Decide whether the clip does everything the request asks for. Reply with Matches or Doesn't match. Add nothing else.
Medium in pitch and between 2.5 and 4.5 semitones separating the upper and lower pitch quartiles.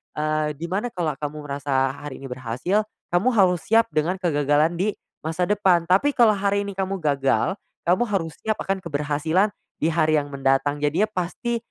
Doesn't match